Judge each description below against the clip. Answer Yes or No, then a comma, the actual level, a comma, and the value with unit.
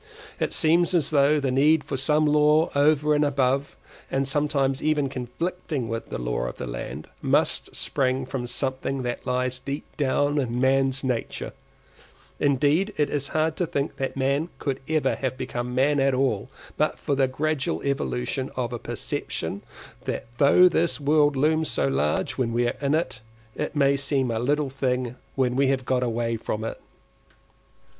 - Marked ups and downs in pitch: No, average, 2.8 semitones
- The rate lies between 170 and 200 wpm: Yes, average, 175 wpm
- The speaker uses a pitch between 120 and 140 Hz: Yes, low, 135 Hz